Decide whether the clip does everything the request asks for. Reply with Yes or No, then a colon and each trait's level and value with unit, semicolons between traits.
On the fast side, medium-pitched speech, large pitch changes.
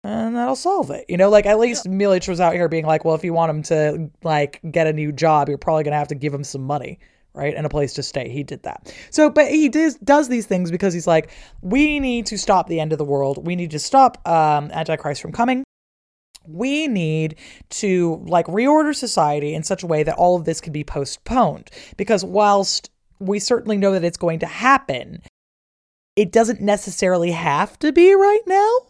Yes: fast, 220 wpm; medium, 175 Hz; wide, 6.6 semitones